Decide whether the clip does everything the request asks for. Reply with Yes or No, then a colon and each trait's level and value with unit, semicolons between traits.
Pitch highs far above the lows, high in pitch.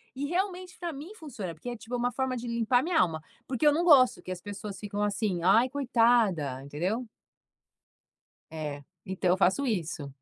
Yes: wide, 6.6 semitones; high, 230 Hz